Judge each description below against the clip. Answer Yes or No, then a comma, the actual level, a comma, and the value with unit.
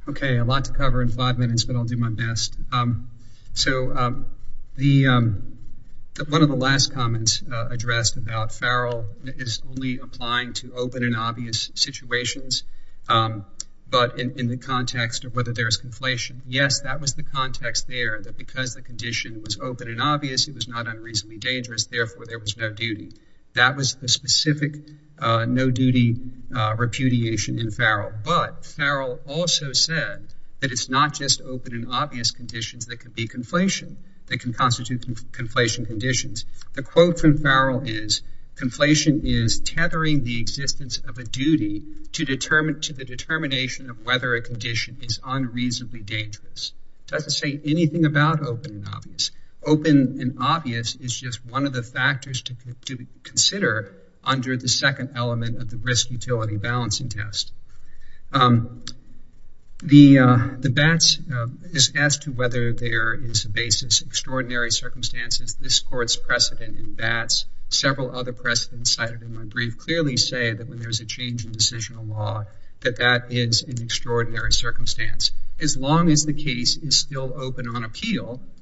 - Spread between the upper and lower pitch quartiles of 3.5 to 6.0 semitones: No, narrow, 2.4 semitones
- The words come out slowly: No, average, 160 wpm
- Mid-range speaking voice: No, low, 125 Hz